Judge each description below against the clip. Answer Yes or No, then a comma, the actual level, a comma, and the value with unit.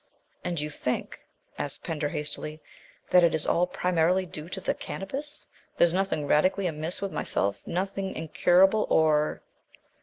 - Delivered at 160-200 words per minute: No, average, 150 wpm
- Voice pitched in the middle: Yes, medium, 175 Hz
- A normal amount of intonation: Yes, average, 3.7 semitones